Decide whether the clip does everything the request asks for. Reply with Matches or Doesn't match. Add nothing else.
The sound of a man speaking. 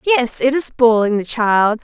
Doesn't match